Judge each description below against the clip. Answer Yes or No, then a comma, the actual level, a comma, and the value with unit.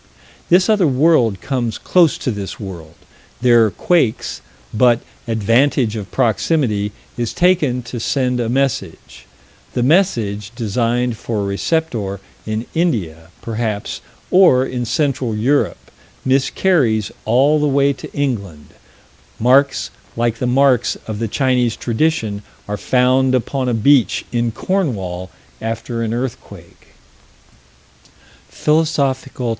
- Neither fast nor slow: No, slow, 120 wpm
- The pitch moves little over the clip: No, average, 4.2 semitones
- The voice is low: Yes, low, 120 Hz